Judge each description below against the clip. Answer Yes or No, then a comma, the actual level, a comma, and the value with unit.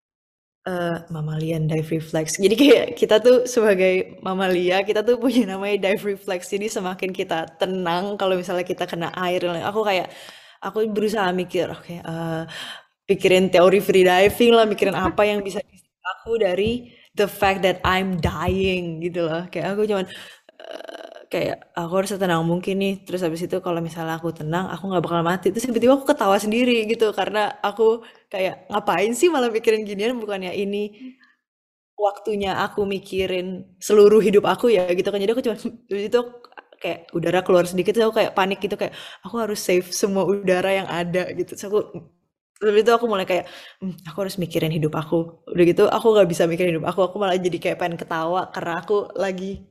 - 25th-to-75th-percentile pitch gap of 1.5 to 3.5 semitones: Yes, average, 2.8 semitones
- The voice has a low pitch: No, high, 190 Hz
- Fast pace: Yes, fast, 180 wpm